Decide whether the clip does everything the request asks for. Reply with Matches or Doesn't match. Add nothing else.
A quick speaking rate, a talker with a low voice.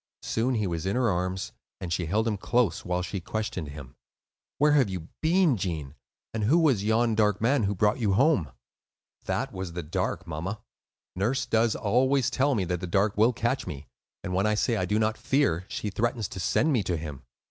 Matches